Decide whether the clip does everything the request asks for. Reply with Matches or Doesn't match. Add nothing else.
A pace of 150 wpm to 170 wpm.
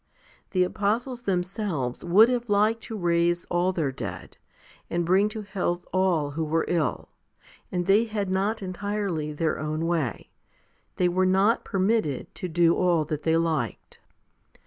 Matches